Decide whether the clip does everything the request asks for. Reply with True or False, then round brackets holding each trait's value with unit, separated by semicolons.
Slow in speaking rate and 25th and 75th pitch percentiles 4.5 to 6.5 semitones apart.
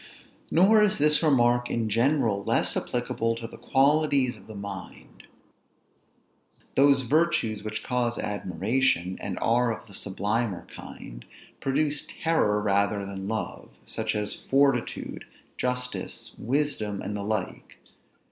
True (125 wpm; 5.0 semitones)